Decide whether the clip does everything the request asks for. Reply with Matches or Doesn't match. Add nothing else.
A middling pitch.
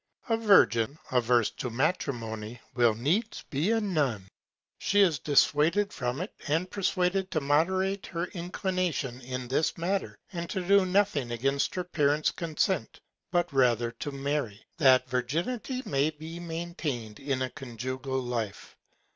Matches